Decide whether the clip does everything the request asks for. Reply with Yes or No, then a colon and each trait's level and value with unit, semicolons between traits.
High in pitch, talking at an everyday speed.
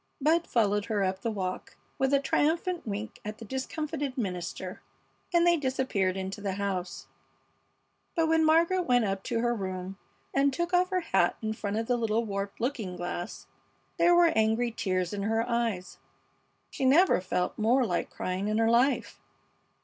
Yes: high, 225 Hz; average, 170 wpm